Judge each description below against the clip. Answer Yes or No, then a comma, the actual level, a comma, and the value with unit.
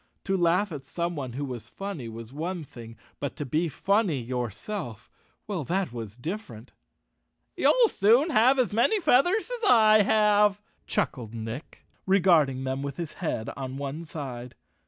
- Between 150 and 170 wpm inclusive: Yes, average, 155 wpm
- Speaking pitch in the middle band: Yes, medium, 160 Hz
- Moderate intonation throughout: No, wide, 8.4 semitones